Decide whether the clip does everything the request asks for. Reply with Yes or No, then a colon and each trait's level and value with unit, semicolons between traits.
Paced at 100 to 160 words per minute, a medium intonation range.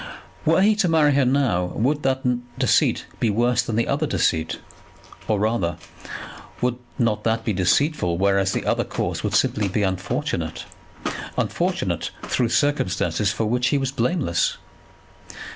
No: average, 150 wpm; wide, 6.1 semitones